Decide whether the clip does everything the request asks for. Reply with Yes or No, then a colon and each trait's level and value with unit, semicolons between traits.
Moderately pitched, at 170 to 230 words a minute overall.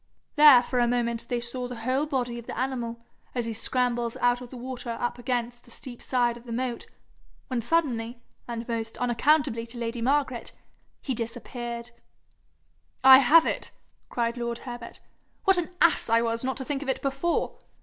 No: high, 245 Hz; average, 180 wpm